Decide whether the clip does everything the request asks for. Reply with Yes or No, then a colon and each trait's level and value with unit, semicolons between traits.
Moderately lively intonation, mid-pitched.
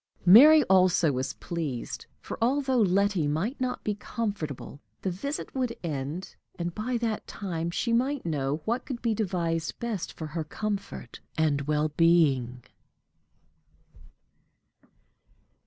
No: wide, 7.0 semitones; medium, 180 Hz